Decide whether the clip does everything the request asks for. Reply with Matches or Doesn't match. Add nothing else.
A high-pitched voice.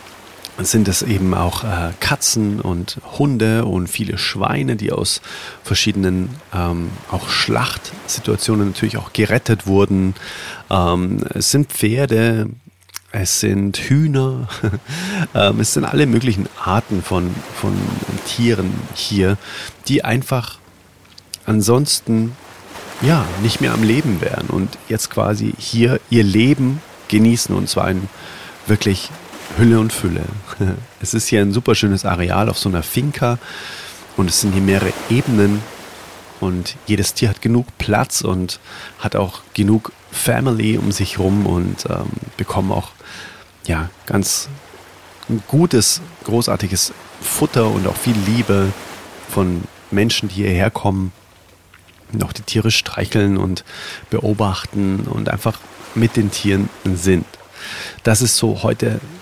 Doesn't match